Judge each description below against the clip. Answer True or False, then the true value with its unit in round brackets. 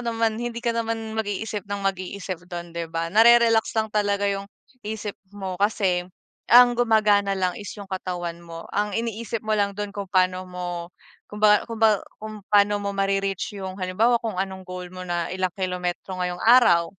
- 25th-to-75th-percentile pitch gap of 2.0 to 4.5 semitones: True (3.0 semitones)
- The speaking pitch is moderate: False (200 Hz)